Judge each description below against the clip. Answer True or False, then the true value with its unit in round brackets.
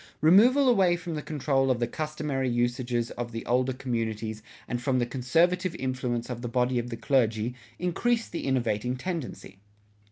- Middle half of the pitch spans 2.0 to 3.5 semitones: False (4.5 semitones)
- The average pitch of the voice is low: True (130 Hz)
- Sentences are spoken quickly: False (165 wpm)